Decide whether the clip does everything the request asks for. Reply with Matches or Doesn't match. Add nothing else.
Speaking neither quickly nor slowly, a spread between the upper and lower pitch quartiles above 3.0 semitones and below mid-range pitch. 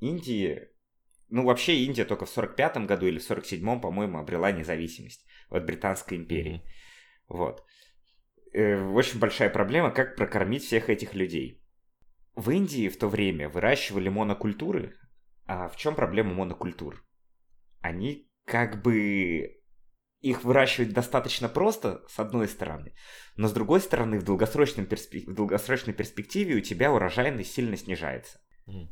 Matches